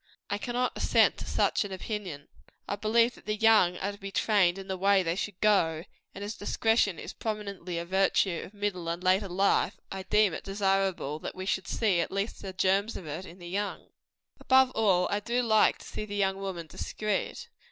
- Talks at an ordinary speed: No, fast, 210 wpm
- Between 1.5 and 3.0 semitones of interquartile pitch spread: Yes, narrow, 2.4 semitones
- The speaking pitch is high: Yes, high, 195 Hz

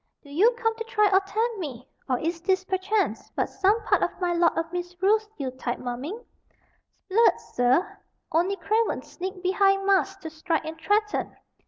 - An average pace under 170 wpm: No, average, 175 wpm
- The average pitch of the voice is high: Yes, very high, 375 Hz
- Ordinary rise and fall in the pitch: Yes, average, 4.2 semitones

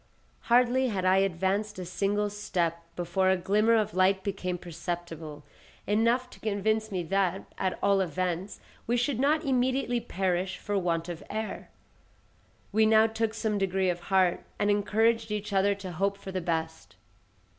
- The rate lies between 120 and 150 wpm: No, average, 160 wpm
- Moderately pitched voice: No, high, 195 Hz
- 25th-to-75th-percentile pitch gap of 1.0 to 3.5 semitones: Yes, average, 3.1 semitones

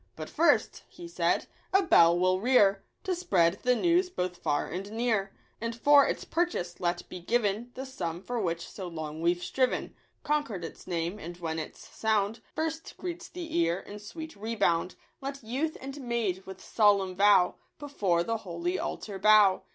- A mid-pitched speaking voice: No, high, 205 Hz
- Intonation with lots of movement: Yes, wide, 6.9 semitones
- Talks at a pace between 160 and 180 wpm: Yes, average, 175 wpm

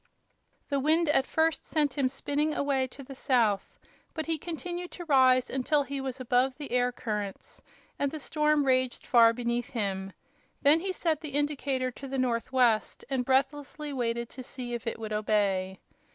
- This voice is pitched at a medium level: No, very high, 265 Hz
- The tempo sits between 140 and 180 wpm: Yes, average, 175 wpm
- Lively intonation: No, average, 3.5 semitones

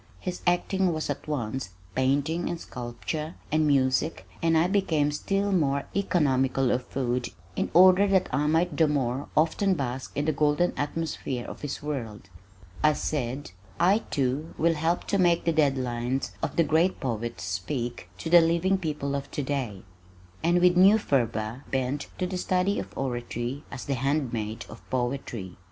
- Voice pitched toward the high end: No, medium, 145 Hz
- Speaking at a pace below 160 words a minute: No, average, 165 wpm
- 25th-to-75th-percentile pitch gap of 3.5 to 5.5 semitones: Yes, average, 4.9 semitones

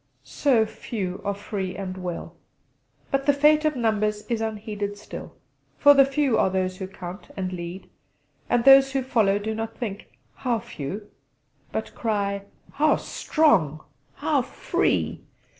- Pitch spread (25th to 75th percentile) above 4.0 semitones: Yes, wide, 5.5 semitones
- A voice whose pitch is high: Yes, high, 215 Hz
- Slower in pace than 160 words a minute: Yes, average, 145 wpm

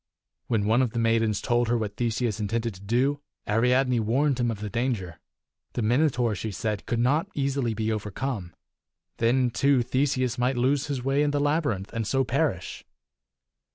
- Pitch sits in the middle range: No, low, 120 Hz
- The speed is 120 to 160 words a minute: No, average, 175 wpm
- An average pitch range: Yes, average, 3.3 semitones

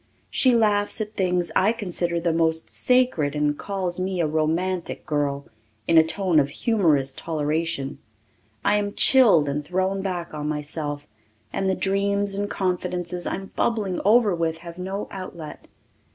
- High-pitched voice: No, medium, 180 Hz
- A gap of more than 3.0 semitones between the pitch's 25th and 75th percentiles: Yes, average, 3.9 semitones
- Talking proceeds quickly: No, average, 155 wpm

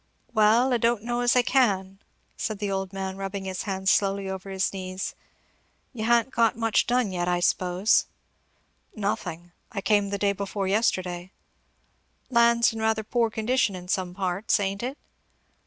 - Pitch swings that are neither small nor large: Yes, average, 3.2 semitones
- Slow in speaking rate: No, average, 165 wpm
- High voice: Yes, high, 200 Hz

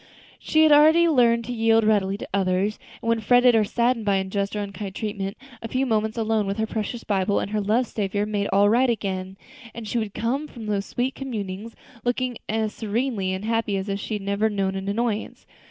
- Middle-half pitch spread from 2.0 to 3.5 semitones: Yes, average, 2.8 semitones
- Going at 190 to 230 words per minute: Yes, fast, 205 wpm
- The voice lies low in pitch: No, high, 215 Hz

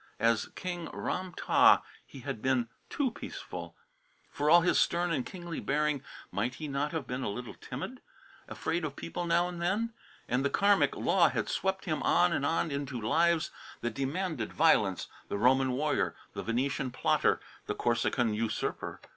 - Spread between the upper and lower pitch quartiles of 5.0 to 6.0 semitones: Yes, wide, 5.4 semitones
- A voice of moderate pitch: Yes, medium, 145 Hz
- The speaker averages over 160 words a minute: Yes, average, 170 wpm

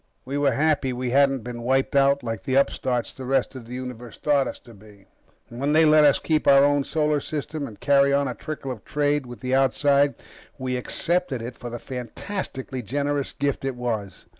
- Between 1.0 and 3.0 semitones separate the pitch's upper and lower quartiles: Yes, average, 2.7 semitones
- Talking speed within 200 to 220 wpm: Yes, fast, 205 wpm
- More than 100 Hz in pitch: Yes, low, 135 Hz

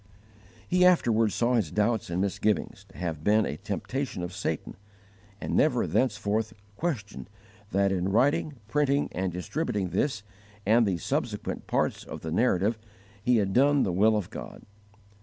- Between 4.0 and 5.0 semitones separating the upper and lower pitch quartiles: Yes, average, 4.5 semitones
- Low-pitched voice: Yes, low, 105 Hz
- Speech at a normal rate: Yes, average, 155 wpm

